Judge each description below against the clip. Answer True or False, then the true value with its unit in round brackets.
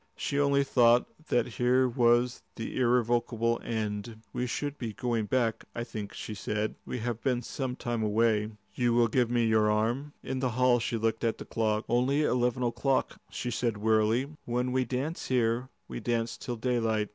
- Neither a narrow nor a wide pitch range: False (2.0 semitones)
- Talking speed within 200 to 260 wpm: False (180 wpm)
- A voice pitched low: True (120 Hz)